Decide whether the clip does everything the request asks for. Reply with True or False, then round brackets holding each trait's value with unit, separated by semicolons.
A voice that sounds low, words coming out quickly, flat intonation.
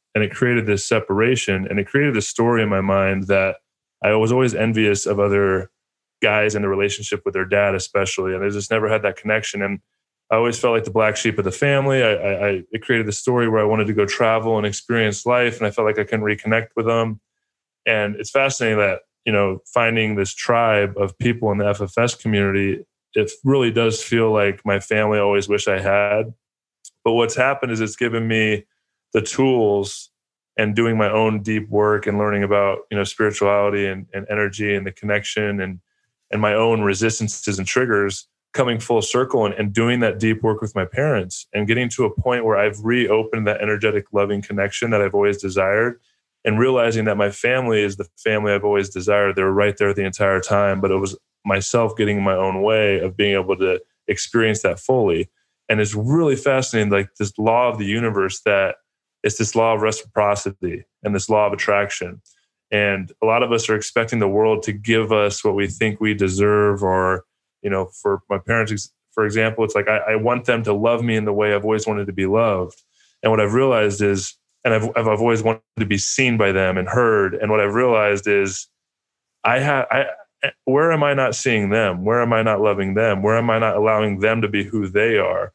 True (105 Hz; 210 wpm; 1.9 semitones)